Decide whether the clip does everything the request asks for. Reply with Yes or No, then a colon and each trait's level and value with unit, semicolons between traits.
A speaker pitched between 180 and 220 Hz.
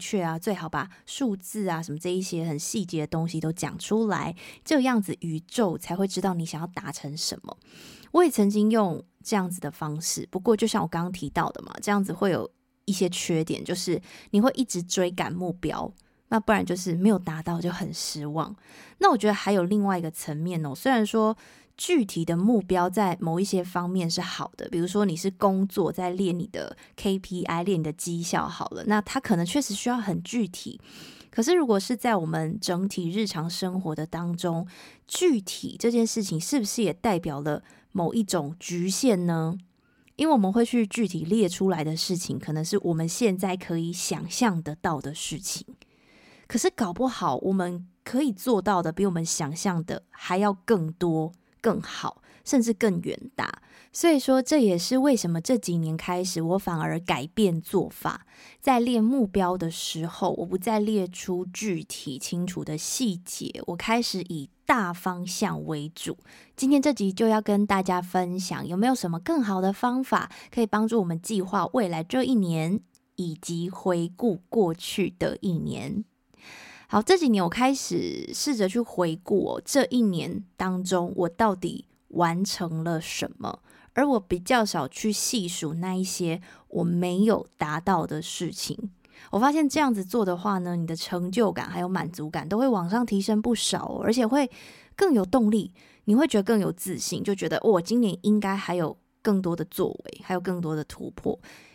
Yes: medium, 185 Hz